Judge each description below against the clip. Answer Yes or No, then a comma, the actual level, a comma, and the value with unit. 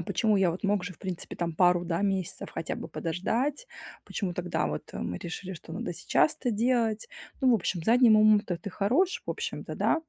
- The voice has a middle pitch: No, high, 195 Hz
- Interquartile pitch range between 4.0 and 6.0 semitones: Yes, average, 4.3 semitones